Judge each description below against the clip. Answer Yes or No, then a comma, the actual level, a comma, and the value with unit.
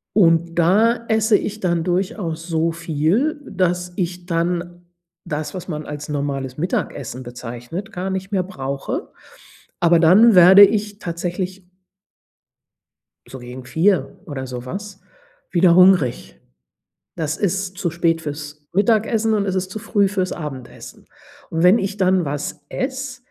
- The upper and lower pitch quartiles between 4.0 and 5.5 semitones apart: Yes, average, 4.3 semitones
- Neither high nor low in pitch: Yes, medium, 175 Hz